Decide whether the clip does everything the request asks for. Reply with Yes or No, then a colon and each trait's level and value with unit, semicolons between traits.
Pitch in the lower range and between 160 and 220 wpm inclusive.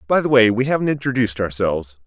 Yes: low, 115 Hz; fast, 205 wpm